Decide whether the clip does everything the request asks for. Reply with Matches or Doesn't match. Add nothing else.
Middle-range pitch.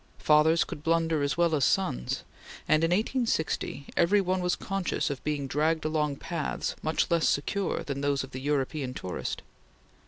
Matches